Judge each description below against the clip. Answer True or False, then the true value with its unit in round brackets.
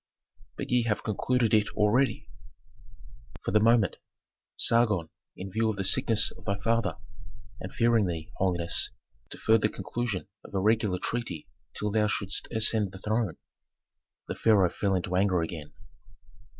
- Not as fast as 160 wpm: True (150 wpm)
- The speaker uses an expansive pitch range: False (3.1 semitones)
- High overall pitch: False (105 Hz)